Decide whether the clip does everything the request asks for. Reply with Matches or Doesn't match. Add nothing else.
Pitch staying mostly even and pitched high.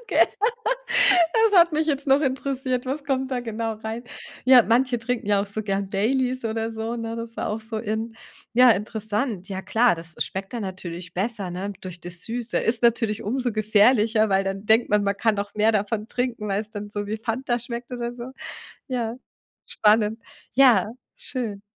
Doesn't match